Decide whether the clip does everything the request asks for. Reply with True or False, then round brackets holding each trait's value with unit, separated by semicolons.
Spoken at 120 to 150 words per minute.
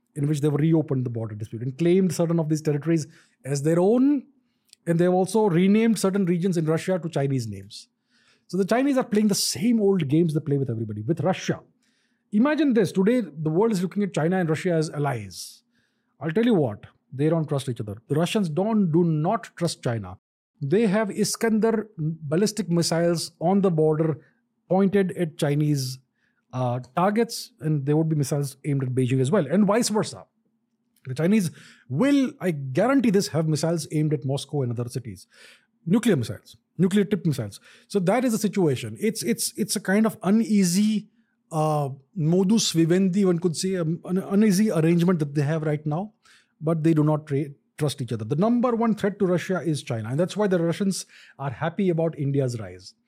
False (190 wpm)